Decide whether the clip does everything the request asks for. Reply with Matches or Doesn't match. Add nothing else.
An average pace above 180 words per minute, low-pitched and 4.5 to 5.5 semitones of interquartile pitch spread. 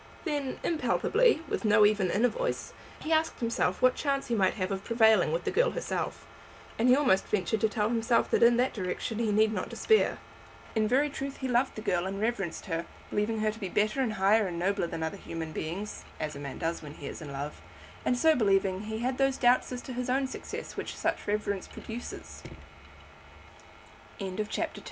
Doesn't match